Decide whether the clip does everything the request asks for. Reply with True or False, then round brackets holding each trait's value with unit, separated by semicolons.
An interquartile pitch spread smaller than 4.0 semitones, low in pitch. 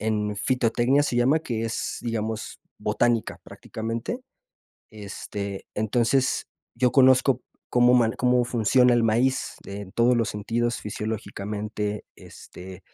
True (2.8 semitones; 115 Hz)